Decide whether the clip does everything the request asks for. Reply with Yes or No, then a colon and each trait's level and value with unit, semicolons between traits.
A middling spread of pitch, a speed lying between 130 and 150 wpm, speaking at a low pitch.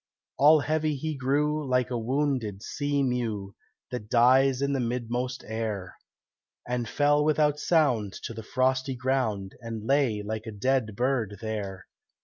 Yes: average, 4.1 semitones; average, 145 wpm; low, 125 Hz